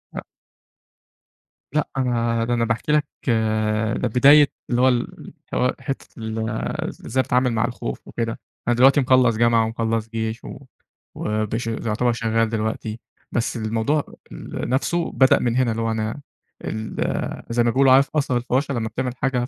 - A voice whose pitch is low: Yes, low, 120 Hz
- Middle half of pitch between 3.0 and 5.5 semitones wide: No, narrow, 2.4 semitones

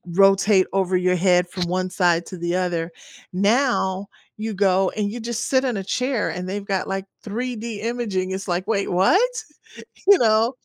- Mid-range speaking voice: No, high, 195 Hz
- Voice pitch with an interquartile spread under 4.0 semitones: Yes, average, 3.4 semitones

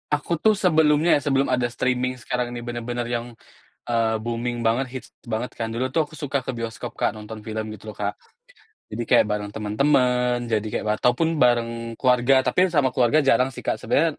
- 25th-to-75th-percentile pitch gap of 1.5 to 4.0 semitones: Yes, average, 2.7 semitones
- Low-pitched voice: Yes, low, 120 Hz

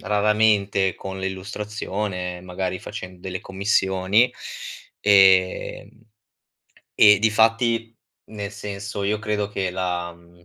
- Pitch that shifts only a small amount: Yes, narrow, 2.2 semitones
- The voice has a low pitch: Yes, low, 100 Hz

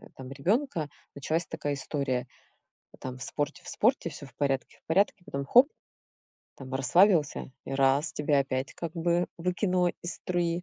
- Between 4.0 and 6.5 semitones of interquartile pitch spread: Yes, average, 4.4 semitones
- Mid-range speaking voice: Yes, medium, 155 Hz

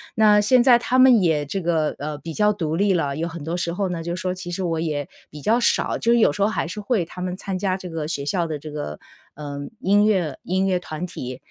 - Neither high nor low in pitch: Yes, medium, 175 Hz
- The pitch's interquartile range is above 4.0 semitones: Yes, average, 4.5 semitones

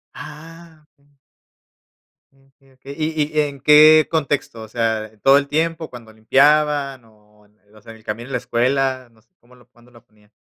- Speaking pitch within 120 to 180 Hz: Yes, low, 135 Hz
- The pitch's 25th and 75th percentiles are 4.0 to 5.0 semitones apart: Yes, average, 4.7 semitones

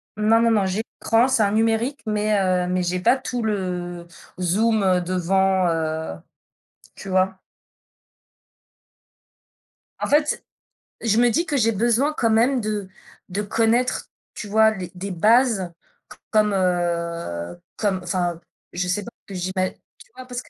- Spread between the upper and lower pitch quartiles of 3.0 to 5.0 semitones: Yes, average, 4.1 semitones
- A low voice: No, high, 200 Hz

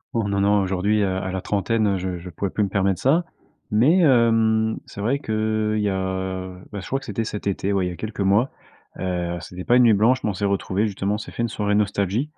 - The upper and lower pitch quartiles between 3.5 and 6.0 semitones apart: No, average, 2.7 semitones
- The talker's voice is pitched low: Yes, low, 105 Hz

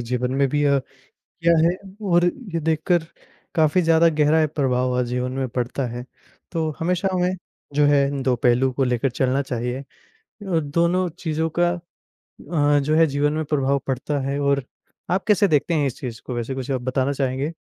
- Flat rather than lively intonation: No, average, 3.9 semitones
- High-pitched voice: No, medium, 145 Hz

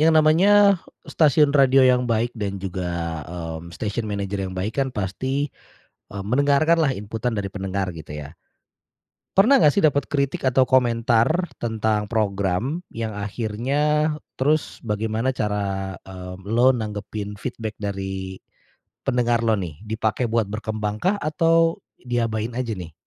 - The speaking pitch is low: Yes, low, 110 Hz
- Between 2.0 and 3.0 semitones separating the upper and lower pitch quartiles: No, average, 5.3 semitones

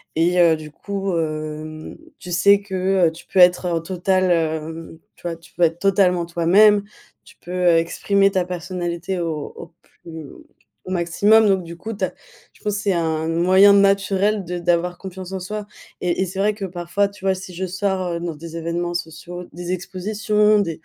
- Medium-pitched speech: Yes, medium, 180 Hz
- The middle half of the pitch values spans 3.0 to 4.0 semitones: No, narrow, 2.6 semitones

